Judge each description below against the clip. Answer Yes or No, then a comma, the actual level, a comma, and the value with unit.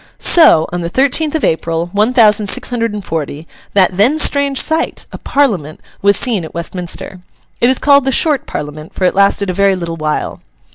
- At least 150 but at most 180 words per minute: No, average, 195 wpm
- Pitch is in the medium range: No, high, 200 Hz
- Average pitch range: No, wide, 7.5 semitones